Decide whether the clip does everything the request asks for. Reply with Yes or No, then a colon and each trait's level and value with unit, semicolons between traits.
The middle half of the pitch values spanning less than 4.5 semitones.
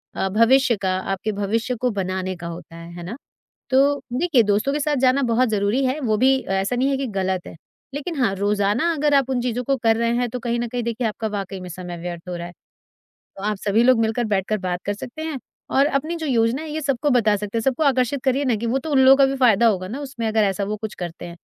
No: average, 5.1 semitones